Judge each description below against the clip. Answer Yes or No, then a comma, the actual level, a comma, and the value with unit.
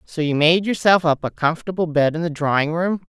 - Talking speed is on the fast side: Yes, fast, 230 wpm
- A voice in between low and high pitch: Yes, medium, 165 Hz